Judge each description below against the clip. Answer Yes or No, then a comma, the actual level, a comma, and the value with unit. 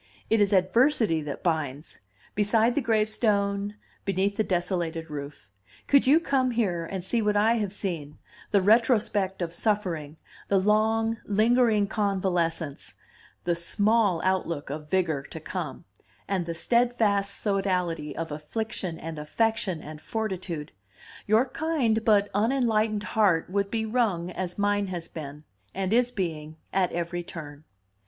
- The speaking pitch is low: No, high, 195 Hz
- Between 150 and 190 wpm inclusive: No, average, 140 wpm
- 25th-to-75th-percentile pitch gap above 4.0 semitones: Yes, average, 4.6 semitones